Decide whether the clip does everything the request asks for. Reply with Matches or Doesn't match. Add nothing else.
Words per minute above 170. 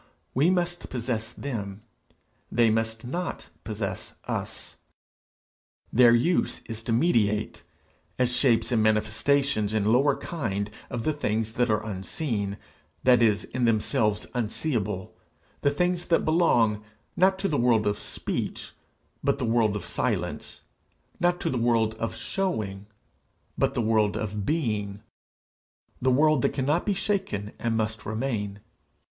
Doesn't match